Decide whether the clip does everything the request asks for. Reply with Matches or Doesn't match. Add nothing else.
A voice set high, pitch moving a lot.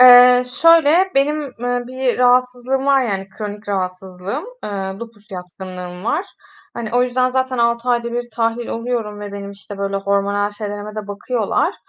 Doesn't match